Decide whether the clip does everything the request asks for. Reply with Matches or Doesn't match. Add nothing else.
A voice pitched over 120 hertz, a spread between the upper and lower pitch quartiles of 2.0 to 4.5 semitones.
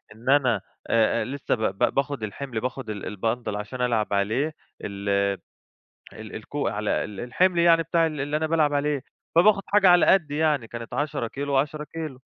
Doesn't match